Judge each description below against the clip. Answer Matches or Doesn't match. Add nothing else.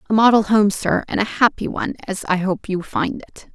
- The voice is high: Matches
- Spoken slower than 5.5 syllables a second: Matches